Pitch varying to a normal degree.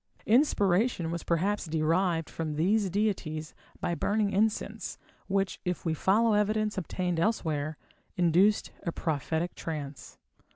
Yes: average, 4.2 semitones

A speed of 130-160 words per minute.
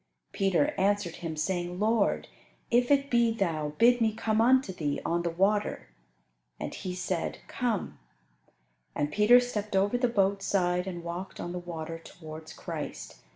Yes: average, 155 wpm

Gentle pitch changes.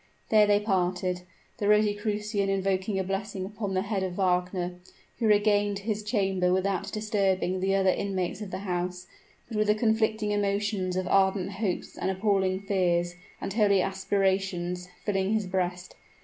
Yes: narrow, 1.9 semitones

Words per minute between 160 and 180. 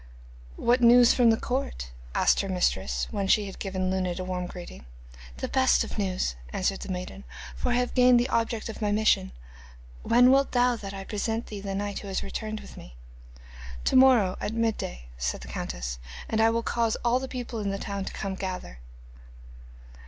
No: average, 200 wpm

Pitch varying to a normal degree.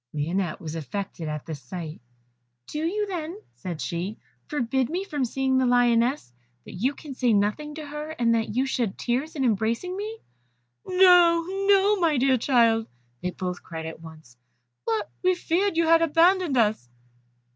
No: wide, 8.8 semitones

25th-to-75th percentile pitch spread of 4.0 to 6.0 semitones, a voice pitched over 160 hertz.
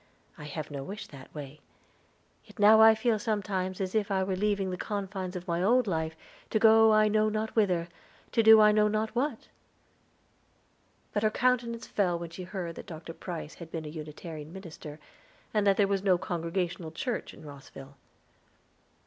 Yes: average, 4.3 semitones; high, 190 Hz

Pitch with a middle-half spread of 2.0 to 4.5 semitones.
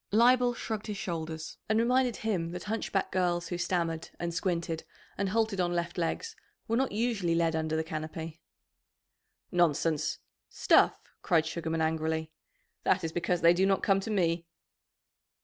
Yes: average, 4.0 semitones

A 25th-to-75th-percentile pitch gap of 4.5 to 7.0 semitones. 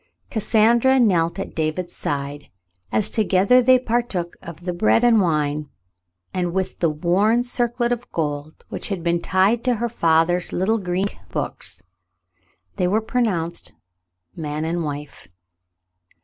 Yes: wide, 5.6 semitones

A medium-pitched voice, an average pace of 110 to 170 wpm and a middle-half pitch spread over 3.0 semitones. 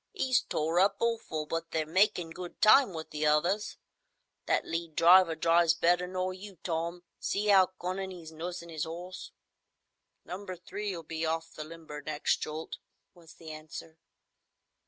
No: medium, 170 Hz; average, 155 wpm; narrow, 2.5 semitones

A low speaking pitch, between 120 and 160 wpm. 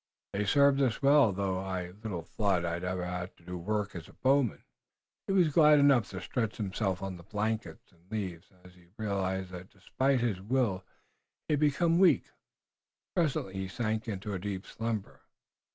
No: low, 100 Hz; average, 180 wpm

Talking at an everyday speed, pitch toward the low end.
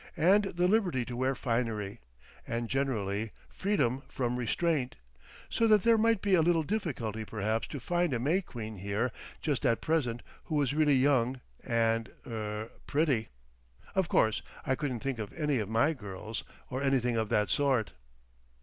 Yes: average, 155 wpm; low, 130 Hz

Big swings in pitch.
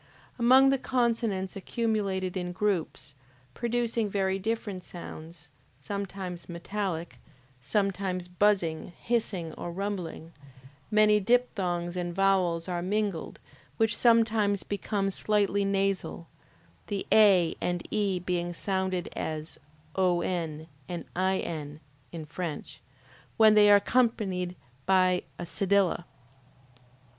No: average, 3.1 semitones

